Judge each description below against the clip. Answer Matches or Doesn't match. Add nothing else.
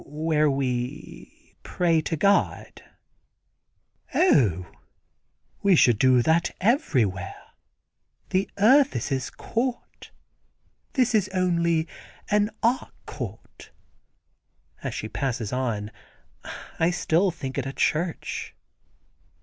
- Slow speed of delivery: Matches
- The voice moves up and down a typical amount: Doesn't match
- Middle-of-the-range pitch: Matches